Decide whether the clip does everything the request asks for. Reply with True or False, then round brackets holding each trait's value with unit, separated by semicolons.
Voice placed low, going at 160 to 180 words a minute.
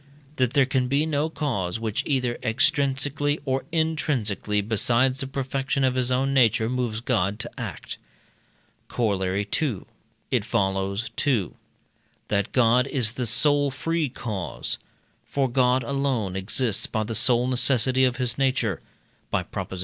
False (125 Hz; 145 wpm)